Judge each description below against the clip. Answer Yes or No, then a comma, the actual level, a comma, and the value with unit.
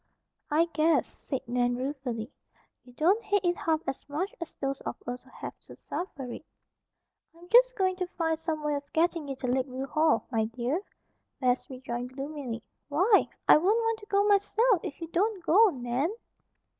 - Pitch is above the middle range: Yes, very high, 305 Hz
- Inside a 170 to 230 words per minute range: Yes, average, 180 wpm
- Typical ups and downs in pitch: No, wide, 6.0 semitones